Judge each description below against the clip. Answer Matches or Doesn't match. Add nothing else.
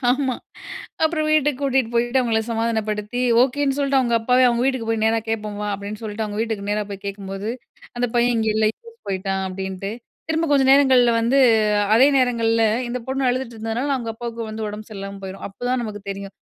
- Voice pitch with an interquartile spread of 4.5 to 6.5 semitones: Doesn't match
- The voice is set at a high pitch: Matches